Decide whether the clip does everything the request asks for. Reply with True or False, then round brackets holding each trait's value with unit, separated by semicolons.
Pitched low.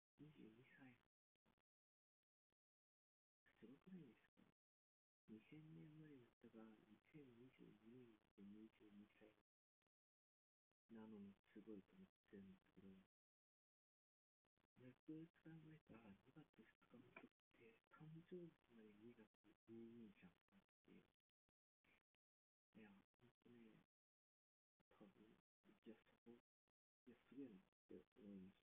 True (115 Hz)